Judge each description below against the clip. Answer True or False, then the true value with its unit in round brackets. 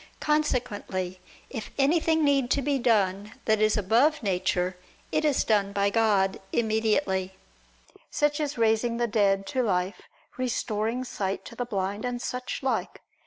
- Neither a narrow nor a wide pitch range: True (4.4 semitones)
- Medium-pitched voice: False (220 Hz)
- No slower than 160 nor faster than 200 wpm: False (145 wpm)